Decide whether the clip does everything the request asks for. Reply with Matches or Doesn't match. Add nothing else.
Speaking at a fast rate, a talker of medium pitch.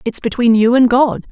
Doesn't match